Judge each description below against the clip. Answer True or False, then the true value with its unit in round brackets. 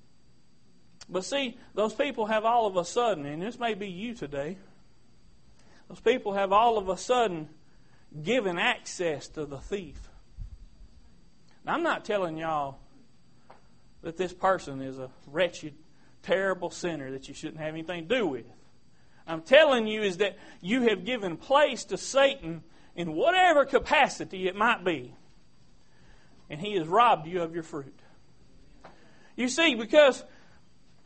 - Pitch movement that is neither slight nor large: False (7.1 semitones)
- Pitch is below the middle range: False (185 Hz)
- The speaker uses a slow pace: False (145 wpm)